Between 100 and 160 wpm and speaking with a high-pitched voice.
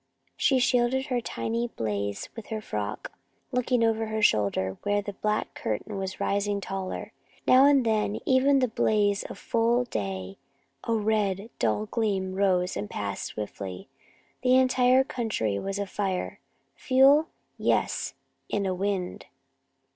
Yes: average, 145 wpm; high, 205 Hz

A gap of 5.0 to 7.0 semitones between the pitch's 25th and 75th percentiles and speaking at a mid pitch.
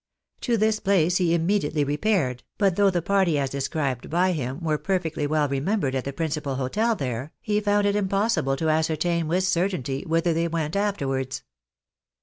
Yes: wide, 5.4 semitones; medium, 165 Hz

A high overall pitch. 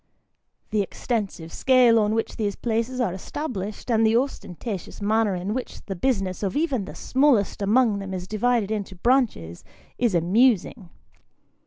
Yes: high, 215 Hz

